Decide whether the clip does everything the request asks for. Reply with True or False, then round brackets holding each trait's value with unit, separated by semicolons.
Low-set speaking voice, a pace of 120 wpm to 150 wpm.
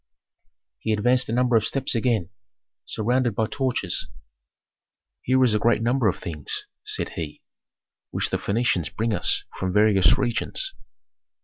True (115 Hz; 140 wpm)